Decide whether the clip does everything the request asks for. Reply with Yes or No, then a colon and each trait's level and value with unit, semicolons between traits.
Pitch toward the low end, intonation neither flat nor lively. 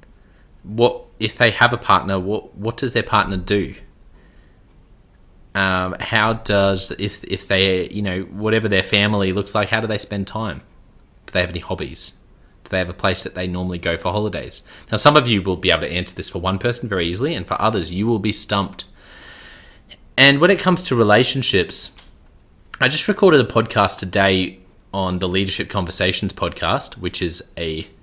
Yes: low, 100 Hz; average, 3.2 semitones